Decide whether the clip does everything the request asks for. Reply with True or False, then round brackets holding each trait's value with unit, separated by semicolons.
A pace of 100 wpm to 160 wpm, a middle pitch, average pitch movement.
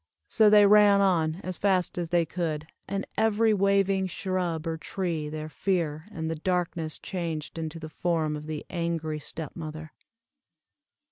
True (155 wpm; 170 Hz; 3.4 semitones)